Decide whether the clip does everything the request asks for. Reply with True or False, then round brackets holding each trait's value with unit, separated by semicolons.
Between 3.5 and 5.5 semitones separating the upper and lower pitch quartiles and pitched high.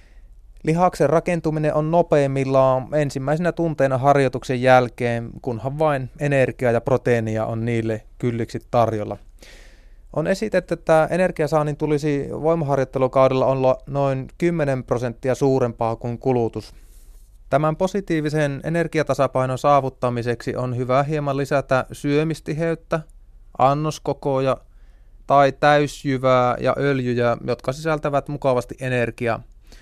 False (3.9 semitones; 135 Hz)